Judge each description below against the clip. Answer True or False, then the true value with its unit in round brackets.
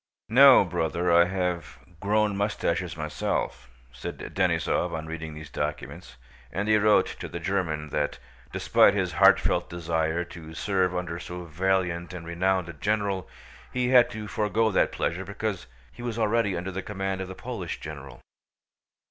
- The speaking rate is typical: True (155 wpm)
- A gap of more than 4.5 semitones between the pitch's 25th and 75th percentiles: False (3.7 semitones)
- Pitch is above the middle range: False (90 Hz)